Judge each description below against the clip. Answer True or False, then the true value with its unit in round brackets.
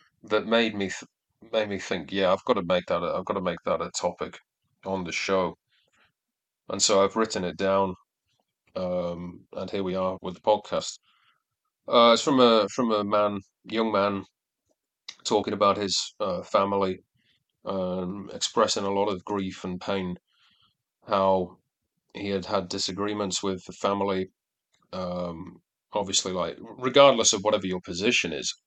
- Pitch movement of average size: False (1.9 semitones)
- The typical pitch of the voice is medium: False (95 Hz)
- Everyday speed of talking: True (160 wpm)